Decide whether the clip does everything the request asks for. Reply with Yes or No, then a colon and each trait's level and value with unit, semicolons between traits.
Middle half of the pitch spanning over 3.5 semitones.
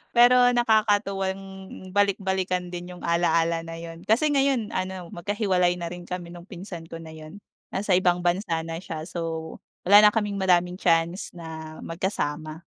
No: average, 3.2 semitones